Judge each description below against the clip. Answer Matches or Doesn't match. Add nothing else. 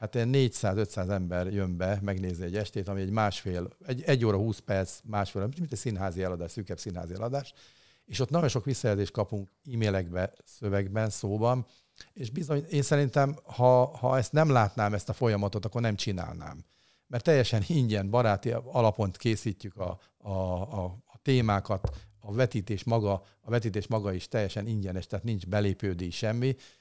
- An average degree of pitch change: Matches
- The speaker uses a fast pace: Matches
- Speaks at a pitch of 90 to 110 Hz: Matches